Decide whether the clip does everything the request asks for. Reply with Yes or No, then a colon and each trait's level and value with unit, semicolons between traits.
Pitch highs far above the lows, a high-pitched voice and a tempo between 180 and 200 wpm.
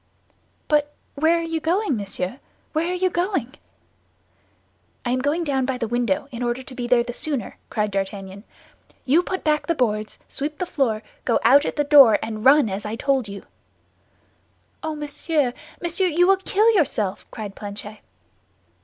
No: wide, 6.3 semitones; very high, 265 Hz; average, 170 wpm